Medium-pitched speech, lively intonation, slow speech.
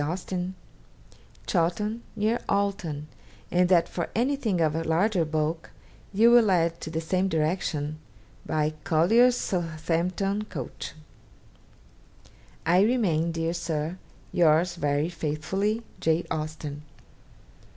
No: medium, 170 Hz; average, 3.8 semitones; slow, 110 wpm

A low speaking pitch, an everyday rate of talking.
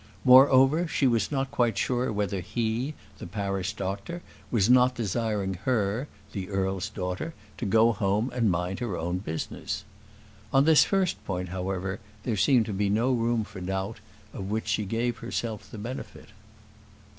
Yes: low, 110 Hz; average, 160 wpm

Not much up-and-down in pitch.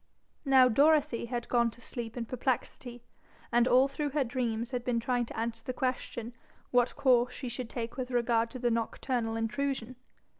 Yes: narrow, 1.8 semitones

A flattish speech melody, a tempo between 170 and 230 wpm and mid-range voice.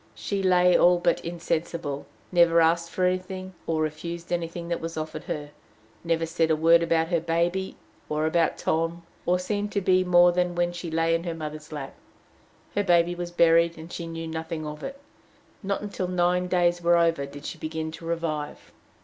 Yes: narrow, 1.5 semitones; average, 190 wpm; medium, 170 Hz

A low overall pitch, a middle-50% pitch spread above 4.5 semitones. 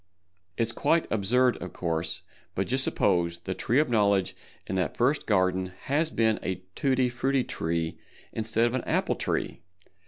Yes: low, 110 Hz; wide, 5.4 semitones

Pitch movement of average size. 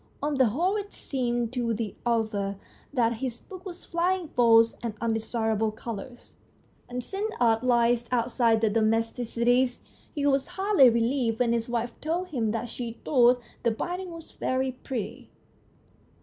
Yes: average, 3.1 semitones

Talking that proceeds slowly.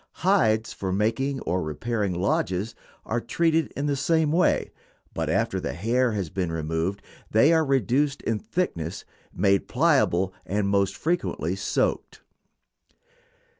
Yes: slow, 130 wpm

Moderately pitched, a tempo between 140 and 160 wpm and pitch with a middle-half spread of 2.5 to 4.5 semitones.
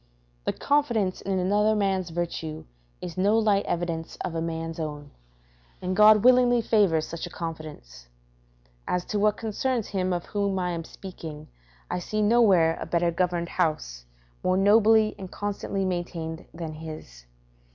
Yes: medium, 180 Hz; average, 150 wpm; average, 4.1 semitones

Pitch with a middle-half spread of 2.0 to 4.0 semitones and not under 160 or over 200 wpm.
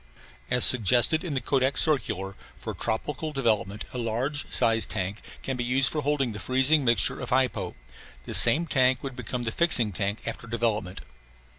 Yes: average, 3.6 semitones; average, 170 wpm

